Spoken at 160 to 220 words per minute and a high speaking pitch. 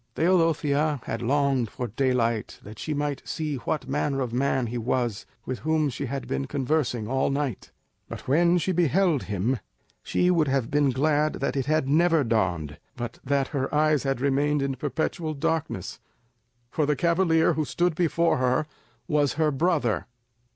No: average, 165 wpm; medium, 140 Hz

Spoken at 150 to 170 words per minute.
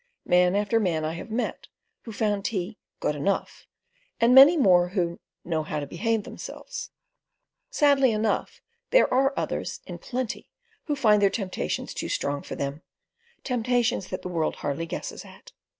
Yes: average, 155 wpm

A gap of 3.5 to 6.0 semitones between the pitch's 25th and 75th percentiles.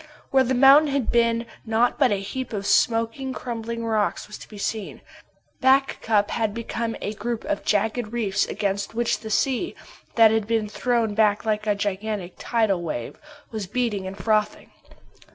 No: narrow, 2.5 semitones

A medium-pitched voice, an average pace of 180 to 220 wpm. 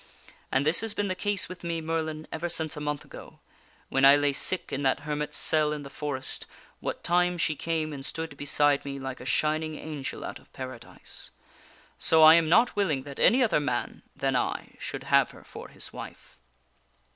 Yes: medium, 155 Hz; average, 200 wpm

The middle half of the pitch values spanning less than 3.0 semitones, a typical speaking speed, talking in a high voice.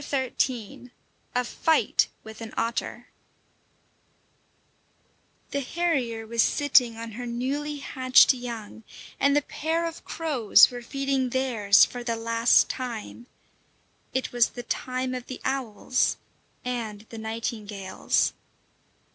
No: narrow, 2.6 semitones; slow, 115 wpm; high, 245 Hz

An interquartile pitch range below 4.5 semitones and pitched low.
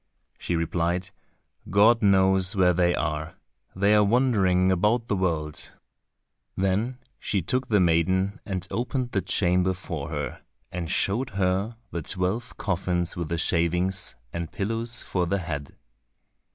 Yes: average, 3.0 semitones; very low, 95 Hz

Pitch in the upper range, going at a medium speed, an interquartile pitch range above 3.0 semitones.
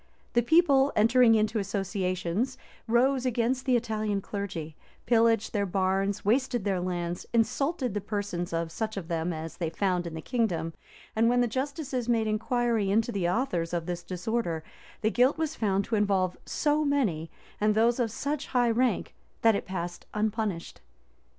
Yes: high, 215 Hz; average, 165 wpm; average, 4.8 semitones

